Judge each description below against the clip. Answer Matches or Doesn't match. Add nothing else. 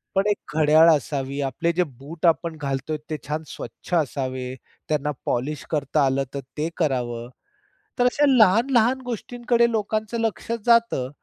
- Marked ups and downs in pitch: Matches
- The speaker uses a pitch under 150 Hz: Doesn't match